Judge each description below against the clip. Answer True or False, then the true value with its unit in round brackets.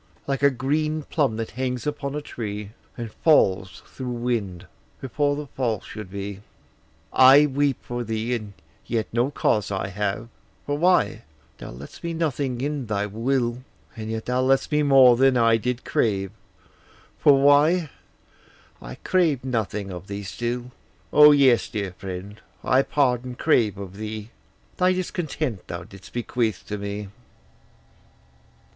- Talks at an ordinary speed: True (150 wpm)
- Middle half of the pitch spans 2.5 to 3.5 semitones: False (5.1 semitones)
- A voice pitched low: True (120 Hz)